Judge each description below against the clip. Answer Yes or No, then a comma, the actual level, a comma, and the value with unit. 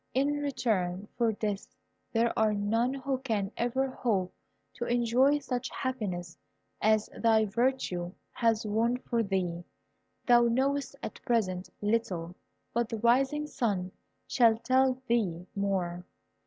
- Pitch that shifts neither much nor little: Yes, average, 4.2 semitones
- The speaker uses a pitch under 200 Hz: No, high, 230 Hz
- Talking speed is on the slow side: Yes, slow, 130 wpm